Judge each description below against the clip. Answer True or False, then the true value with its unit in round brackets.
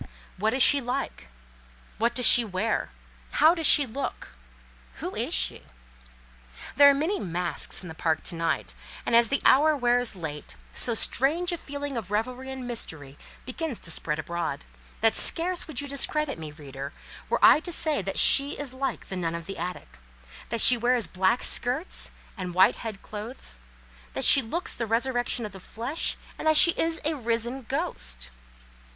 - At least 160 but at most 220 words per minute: True (180 wpm)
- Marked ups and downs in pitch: True (7.3 semitones)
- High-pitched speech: True (235 Hz)